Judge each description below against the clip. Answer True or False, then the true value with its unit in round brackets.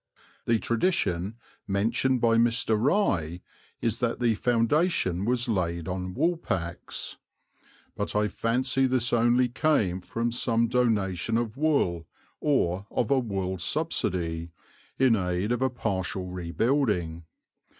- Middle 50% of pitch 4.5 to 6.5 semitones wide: True (5.3 semitones)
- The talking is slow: True (120 wpm)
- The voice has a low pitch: True (115 Hz)